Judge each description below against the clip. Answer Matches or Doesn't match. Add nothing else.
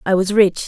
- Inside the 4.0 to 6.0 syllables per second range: Matches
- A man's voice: Doesn't match